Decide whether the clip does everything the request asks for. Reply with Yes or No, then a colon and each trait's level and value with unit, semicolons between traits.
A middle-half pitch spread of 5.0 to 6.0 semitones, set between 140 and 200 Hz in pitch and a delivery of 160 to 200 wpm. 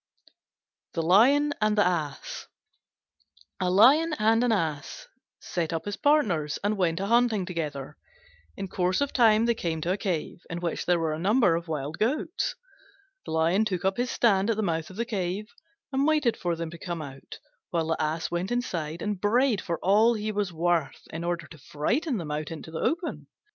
Yes: wide, 5.5 semitones; medium, 185 Hz; average, 195 wpm